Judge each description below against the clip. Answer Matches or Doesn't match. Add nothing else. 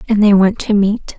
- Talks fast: Matches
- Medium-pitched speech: Doesn't match